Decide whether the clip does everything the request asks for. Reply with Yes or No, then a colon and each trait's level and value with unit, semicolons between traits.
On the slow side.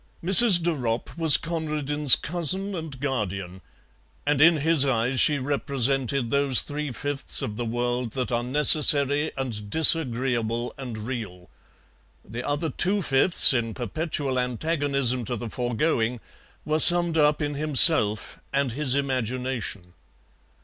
Yes: slow, 130 wpm